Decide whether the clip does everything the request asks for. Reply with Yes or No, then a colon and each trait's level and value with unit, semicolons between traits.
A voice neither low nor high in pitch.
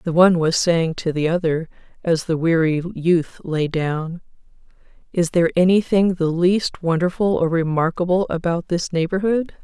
Yes: medium, 170 Hz